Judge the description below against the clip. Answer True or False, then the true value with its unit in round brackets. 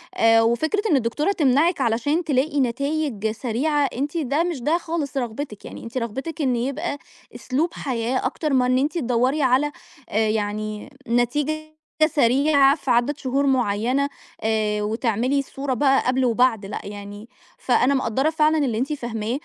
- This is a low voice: False (260 Hz)